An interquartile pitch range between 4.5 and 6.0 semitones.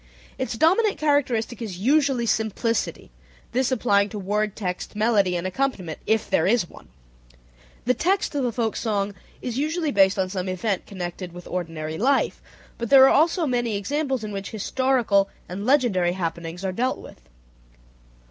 Yes: wide, 5.6 semitones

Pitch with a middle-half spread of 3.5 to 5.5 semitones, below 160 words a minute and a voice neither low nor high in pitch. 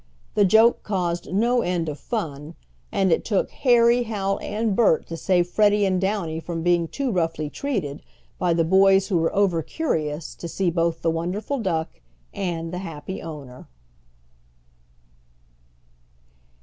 Yes: average, 3.9 semitones; average, 150 wpm; medium, 180 Hz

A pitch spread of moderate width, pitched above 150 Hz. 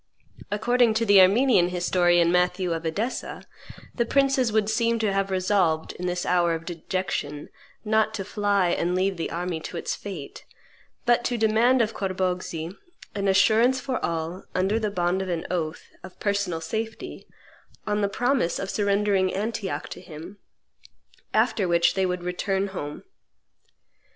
Yes: average, 3.6 semitones; high, 190 Hz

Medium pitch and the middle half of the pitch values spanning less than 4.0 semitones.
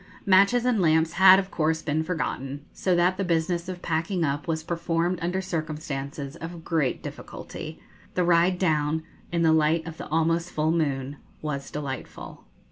Yes: medium, 165 Hz; narrow, 2.5 semitones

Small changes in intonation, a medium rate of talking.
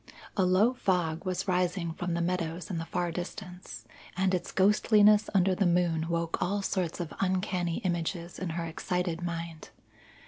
Yes: narrow, 2.0 semitones; average, 165 wpm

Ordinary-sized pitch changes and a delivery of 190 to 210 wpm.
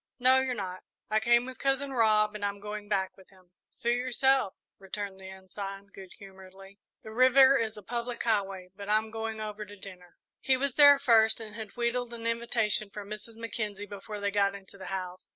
Yes: average, 3.2 semitones; average, 200 wpm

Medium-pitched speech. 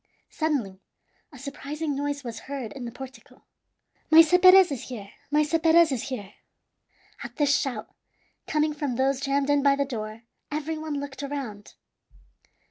No: very high, 280 Hz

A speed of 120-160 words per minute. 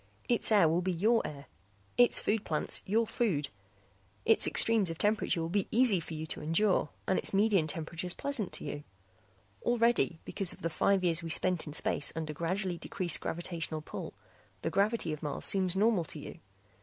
No: average, 185 wpm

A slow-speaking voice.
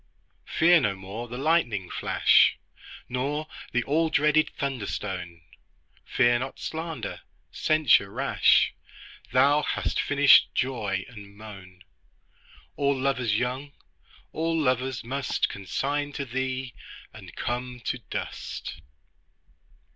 Yes: slow, 110 wpm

